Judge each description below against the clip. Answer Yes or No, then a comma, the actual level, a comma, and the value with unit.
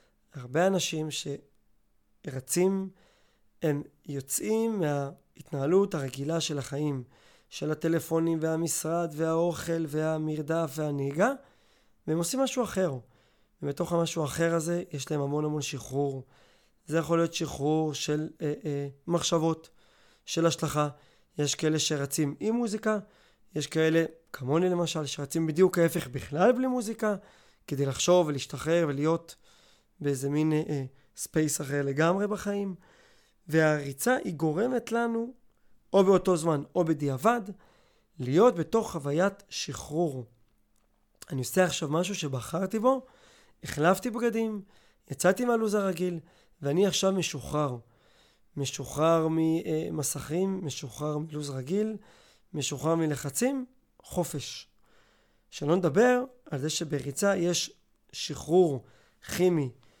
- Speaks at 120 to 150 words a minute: No, average, 105 wpm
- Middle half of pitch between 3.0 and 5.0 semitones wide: Yes, average, 4.3 semitones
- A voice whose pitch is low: No, medium, 160 Hz